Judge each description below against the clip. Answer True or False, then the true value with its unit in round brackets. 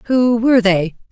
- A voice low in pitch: False (220 Hz)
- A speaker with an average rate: True (160 wpm)